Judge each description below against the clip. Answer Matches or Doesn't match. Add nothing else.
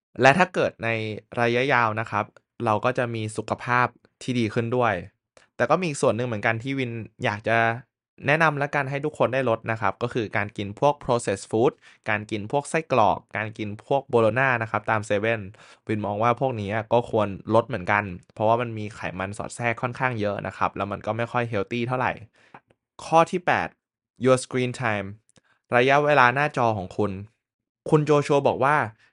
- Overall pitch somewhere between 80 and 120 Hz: Matches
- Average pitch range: Matches